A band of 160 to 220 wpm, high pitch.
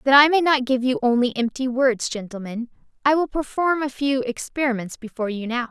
Yes: average, 200 wpm; very high, 255 Hz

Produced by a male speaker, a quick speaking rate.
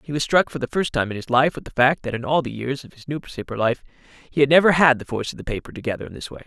Yes: male; fast, 325 wpm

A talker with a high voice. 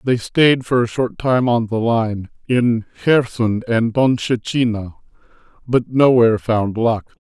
No: low, 115 Hz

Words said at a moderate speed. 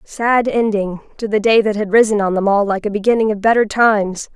No: fast, 235 wpm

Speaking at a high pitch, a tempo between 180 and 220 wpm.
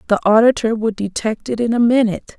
Yes: high, 225 Hz; average, 200 wpm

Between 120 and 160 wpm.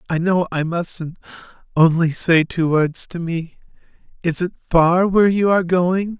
Yes: average, 155 wpm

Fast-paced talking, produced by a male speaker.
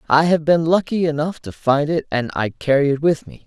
Yes: fast, 240 wpm; male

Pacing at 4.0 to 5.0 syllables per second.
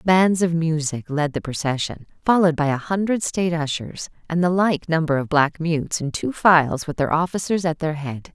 No: 5.2 syllables/s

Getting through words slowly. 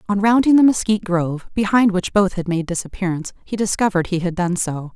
No: fast, 205 wpm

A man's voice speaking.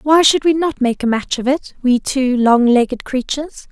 No: female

